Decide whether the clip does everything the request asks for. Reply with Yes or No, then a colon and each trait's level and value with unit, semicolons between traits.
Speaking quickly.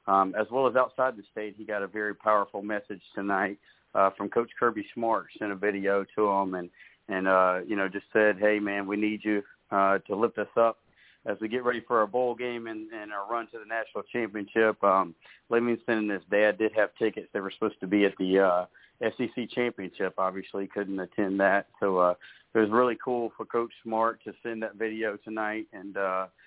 Yes: fast, 215 wpm